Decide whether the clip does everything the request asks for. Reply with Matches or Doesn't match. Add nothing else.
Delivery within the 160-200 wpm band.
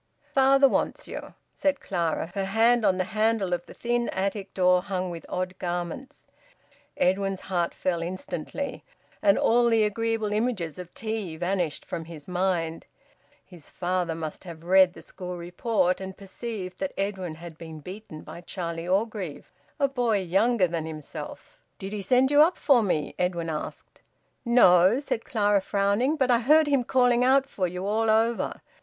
Matches